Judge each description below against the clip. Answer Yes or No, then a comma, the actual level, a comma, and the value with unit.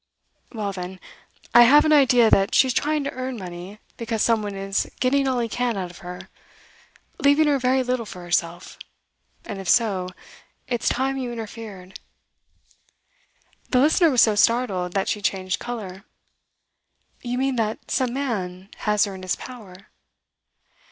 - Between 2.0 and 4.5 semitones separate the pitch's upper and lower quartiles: No, average, 4.9 semitones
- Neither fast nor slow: Yes, average, 160 wpm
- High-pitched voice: Yes, high, 225 Hz